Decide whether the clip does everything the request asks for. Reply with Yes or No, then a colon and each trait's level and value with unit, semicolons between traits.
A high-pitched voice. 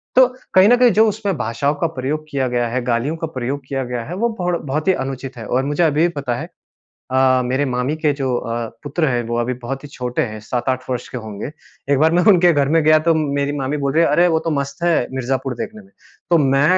No: medium, 140 Hz